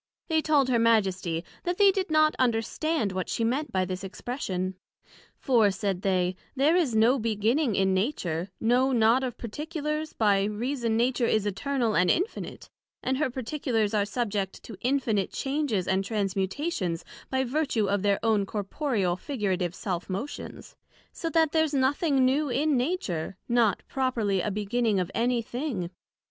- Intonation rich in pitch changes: Yes, wide, 5.9 semitones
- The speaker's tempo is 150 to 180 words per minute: Yes, average, 155 wpm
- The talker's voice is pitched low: No, high, 230 Hz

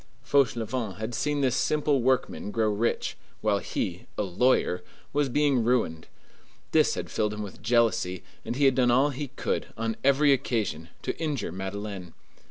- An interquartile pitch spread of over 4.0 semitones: Yes, average, 4.8 semitones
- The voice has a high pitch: No, low, 115 Hz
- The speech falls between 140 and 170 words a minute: Yes, average, 165 wpm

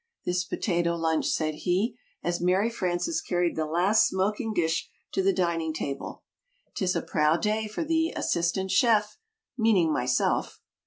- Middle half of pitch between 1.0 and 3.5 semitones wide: No, average, 4.0 semitones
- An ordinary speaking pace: Yes, average, 150 wpm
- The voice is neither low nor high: Yes, medium, 180 Hz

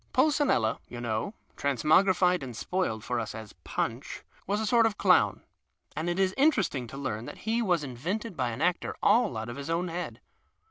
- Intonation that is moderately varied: No, wide, 8.6 semitones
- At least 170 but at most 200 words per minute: Yes, average, 195 wpm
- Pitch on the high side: No, medium, 170 Hz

